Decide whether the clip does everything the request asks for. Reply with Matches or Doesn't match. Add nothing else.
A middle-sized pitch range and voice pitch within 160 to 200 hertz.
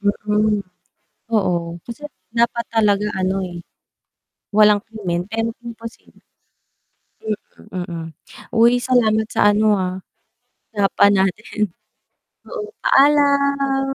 Doesn't match